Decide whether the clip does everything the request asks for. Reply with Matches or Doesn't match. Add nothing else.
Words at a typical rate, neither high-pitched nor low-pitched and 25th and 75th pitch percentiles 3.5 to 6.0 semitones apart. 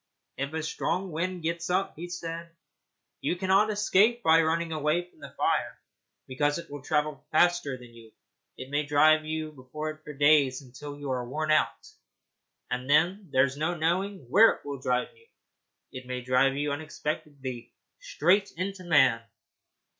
Matches